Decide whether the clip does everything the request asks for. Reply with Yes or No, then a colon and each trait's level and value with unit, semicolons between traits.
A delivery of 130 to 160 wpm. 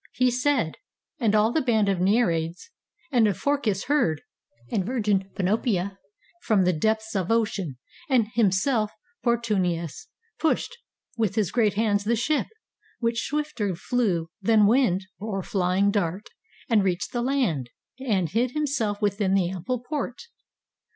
Yes: average, 140 wpm